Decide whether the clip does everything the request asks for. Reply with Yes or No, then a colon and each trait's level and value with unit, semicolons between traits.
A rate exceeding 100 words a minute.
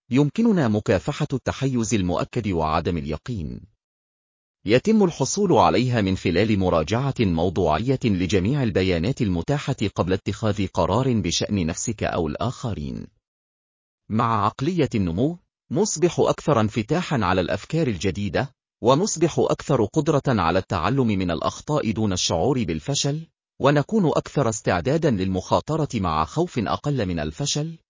Yes: average, 110 wpm